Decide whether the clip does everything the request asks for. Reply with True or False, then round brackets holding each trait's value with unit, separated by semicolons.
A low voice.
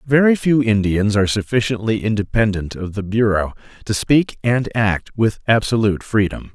True (110 Hz)